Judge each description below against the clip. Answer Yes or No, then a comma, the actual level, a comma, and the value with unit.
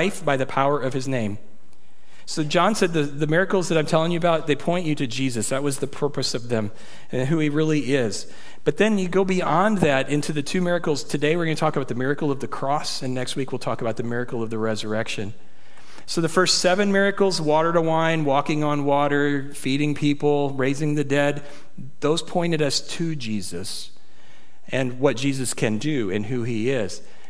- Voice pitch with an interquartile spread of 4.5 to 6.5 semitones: No, average, 3.6 semitones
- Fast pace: Yes, fast, 210 wpm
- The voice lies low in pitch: No, medium, 145 Hz